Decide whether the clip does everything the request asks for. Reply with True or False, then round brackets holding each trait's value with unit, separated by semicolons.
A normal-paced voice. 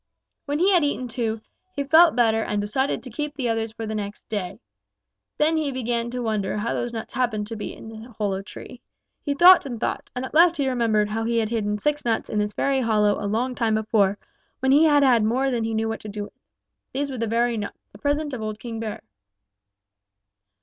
False (230 wpm)